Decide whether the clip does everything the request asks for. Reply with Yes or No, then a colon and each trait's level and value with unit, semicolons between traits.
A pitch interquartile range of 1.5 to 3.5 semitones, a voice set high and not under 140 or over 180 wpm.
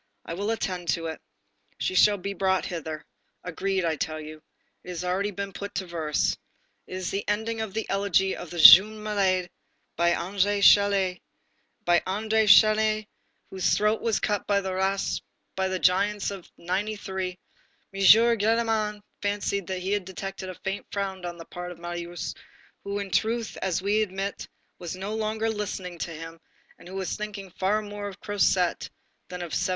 Yes: narrow, 2.4 semitones; high, 195 Hz; average, 175 wpm